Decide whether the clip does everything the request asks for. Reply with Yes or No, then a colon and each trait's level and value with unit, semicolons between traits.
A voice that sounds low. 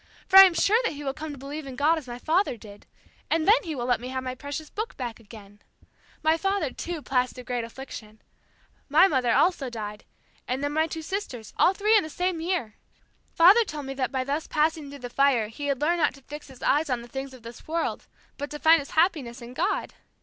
No: very high, 285 Hz